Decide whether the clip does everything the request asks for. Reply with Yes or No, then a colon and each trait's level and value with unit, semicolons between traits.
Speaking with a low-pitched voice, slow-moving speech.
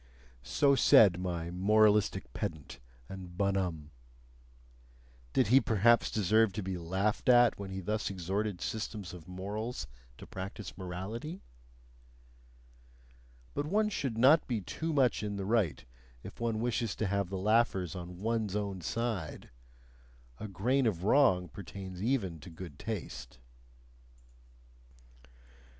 Yes: low, 100 Hz; slow, 130 wpm